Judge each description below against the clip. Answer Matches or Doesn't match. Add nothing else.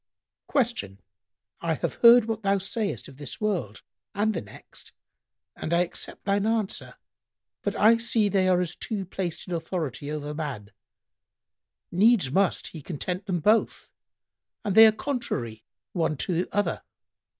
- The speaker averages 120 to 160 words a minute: Matches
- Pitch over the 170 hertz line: Matches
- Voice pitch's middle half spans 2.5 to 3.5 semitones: Doesn't match